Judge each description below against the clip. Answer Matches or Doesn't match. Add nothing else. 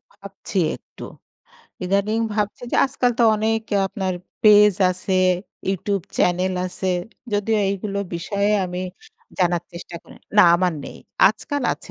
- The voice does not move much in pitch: Matches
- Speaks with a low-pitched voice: Doesn't match